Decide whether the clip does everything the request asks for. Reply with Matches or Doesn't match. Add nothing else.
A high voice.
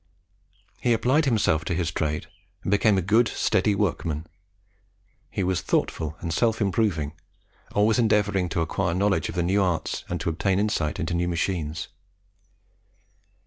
Doesn't match